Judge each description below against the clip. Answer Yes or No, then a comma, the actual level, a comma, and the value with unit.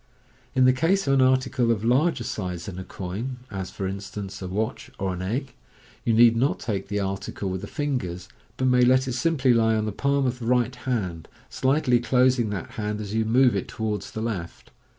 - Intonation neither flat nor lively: Yes, average, 4.6 semitones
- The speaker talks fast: Yes, fast, 220 wpm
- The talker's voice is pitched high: No, low, 115 Hz